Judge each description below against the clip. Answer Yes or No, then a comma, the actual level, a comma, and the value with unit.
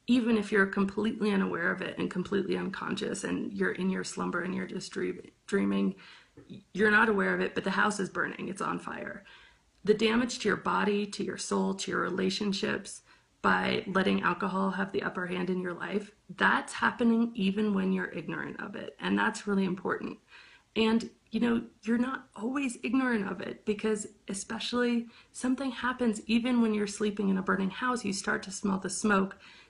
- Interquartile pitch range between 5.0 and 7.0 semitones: No, average, 2.9 semitones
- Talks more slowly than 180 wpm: No, average, 190 wpm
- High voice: Yes, high, 205 Hz